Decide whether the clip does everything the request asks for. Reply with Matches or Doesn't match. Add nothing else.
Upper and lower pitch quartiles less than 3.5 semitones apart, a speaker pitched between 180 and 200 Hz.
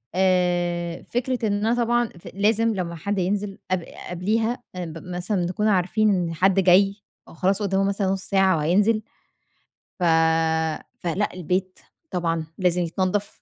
Matches